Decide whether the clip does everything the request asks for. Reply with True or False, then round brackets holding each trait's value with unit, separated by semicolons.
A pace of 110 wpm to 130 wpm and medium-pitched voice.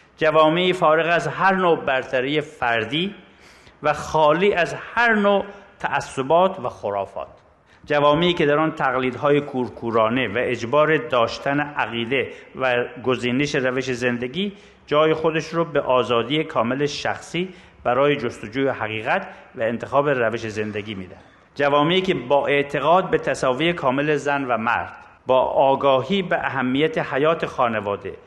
True (125 wpm; 145 Hz)